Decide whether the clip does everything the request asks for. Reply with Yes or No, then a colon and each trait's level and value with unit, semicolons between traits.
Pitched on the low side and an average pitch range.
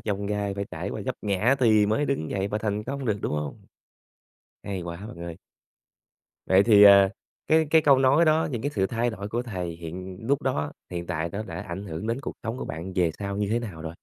Yes: low, 100 Hz; average, 4.5 semitones